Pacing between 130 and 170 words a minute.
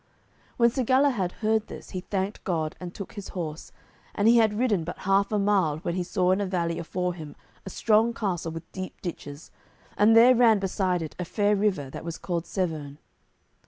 No: average, 200 wpm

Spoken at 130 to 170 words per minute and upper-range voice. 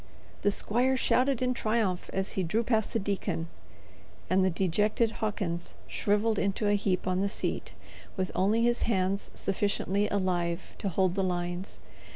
Yes: average, 160 wpm; high, 200 Hz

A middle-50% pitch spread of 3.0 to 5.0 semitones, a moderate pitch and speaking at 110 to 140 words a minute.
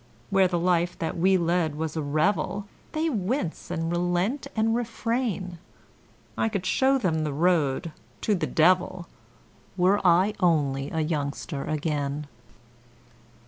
Yes: average, 4.0 semitones; medium, 175 Hz; slow, 135 wpm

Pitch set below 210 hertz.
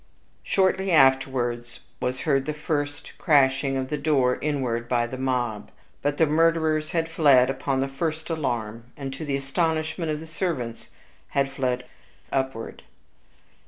Yes: low, 135 Hz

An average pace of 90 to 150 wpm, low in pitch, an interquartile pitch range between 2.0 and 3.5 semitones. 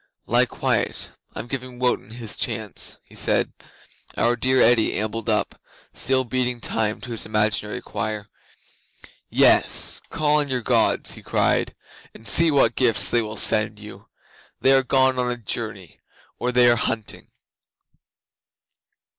Yes: average, 145 wpm; low, 120 Hz; average, 2.9 semitones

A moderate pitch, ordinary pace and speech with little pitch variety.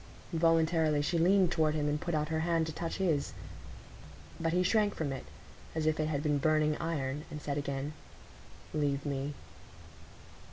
Yes: medium, 155 Hz; average, 170 wpm; narrow, 2.1 semitones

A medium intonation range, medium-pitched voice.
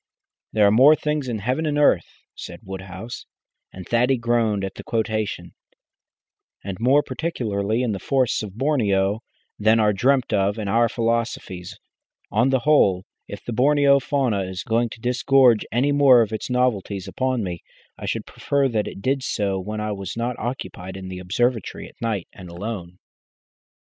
No: average, 4.5 semitones; low, 115 Hz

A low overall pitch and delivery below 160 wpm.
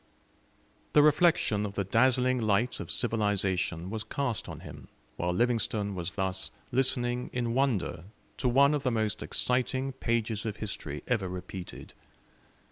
Yes: low, 115 Hz; average, 140 wpm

